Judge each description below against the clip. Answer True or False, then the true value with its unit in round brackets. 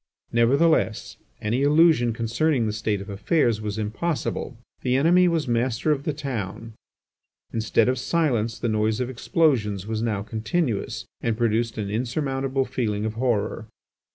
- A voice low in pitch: True (115 Hz)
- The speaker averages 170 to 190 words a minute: False (145 wpm)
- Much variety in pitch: False (4.0 semitones)